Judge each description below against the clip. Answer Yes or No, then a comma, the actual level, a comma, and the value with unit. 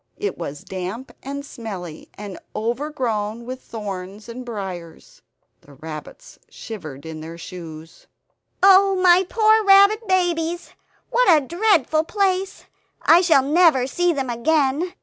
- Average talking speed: No, slow, 130 wpm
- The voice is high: Yes, very high, 265 Hz